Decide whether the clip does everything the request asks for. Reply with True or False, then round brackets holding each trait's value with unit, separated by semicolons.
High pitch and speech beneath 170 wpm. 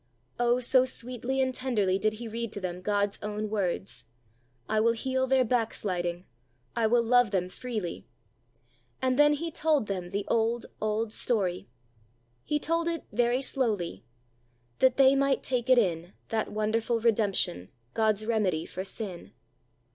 True (225 Hz; 155 wpm)